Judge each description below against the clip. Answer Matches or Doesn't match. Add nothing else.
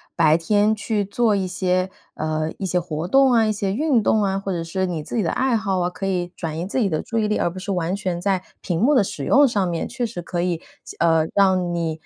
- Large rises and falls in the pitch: Doesn't match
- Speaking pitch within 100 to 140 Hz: Doesn't match